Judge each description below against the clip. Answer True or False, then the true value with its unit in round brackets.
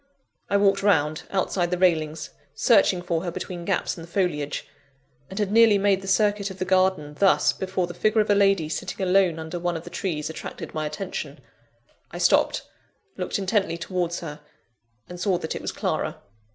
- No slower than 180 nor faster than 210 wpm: True (190 wpm)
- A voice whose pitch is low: False (185 Hz)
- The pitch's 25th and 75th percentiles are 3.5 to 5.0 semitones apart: False (2.9 semitones)